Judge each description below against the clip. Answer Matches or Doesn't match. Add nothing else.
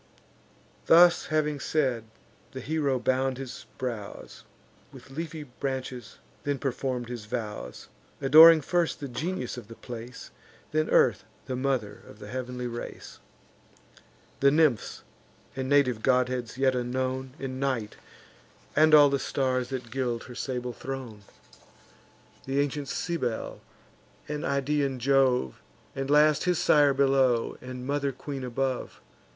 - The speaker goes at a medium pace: Doesn't match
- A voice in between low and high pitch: Doesn't match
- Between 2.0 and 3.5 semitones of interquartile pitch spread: Matches